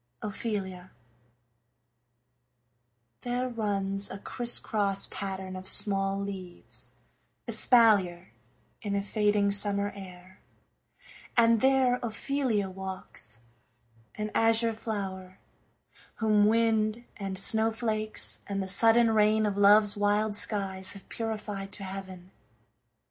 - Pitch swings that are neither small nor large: No, narrow, 2.3 semitones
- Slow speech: Yes, slow, 100 wpm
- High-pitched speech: Yes, high, 205 Hz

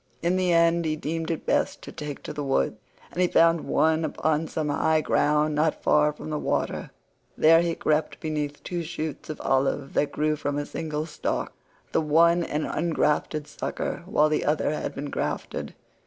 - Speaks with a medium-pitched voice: Yes, medium, 155 Hz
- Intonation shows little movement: Yes, narrow, 1.6 semitones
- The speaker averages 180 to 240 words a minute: Yes, average, 185 wpm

